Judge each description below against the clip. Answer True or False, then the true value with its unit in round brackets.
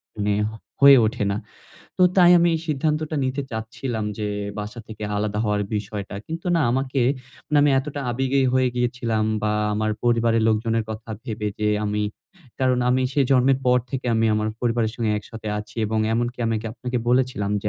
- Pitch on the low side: True (115 Hz)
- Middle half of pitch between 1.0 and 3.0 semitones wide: False (3.4 semitones)